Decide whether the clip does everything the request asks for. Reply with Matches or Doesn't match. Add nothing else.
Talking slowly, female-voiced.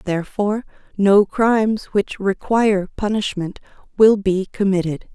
Matches